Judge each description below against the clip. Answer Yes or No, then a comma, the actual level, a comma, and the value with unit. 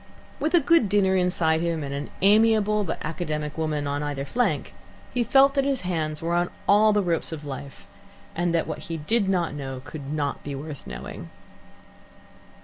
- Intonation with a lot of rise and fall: Yes, wide, 5.8 semitones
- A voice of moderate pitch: Yes, medium, 165 Hz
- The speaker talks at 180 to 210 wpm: Yes, average, 185 wpm